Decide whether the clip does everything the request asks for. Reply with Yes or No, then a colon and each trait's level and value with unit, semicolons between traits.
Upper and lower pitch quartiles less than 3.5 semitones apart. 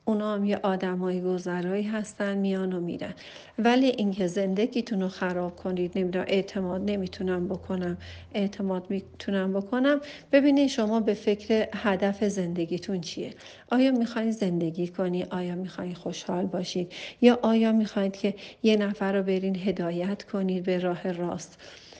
Yes: narrow, 2.5 semitones